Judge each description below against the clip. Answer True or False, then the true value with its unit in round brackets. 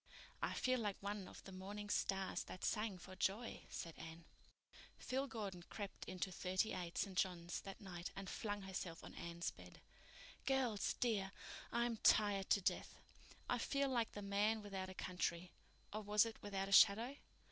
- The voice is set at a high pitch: True (200 Hz)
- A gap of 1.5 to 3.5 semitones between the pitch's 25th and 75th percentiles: True (2.7 semitones)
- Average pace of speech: True (170 wpm)